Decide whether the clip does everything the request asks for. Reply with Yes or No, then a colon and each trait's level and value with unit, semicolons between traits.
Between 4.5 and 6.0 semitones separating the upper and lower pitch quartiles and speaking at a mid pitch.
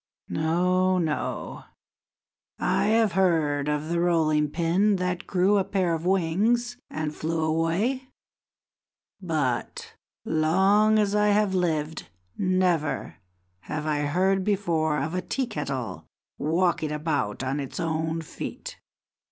No: average, 3.7 semitones; medium, 170 Hz